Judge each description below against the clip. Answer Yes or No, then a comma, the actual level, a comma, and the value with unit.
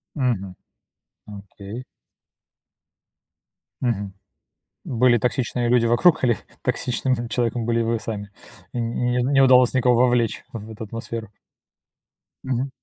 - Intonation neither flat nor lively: No, narrow, 2.0 semitones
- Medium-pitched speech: No, low, 120 Hz